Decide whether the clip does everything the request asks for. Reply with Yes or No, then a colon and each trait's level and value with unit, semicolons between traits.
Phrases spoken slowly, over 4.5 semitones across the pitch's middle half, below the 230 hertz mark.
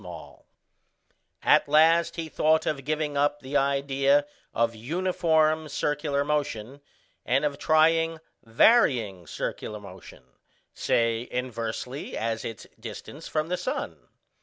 Yes: slow, 115 wpm; average, 5.1 semitones; medium, 140 Hz